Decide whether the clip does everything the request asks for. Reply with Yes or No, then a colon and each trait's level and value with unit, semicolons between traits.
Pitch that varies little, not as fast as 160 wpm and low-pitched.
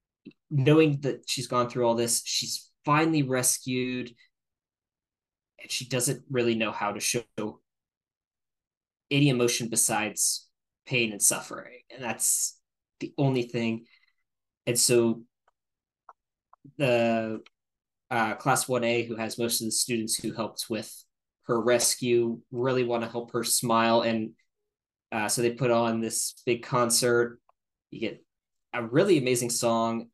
Yes: narrow, 1.7 semitones; slow, 135 wpm; low, 120 Hz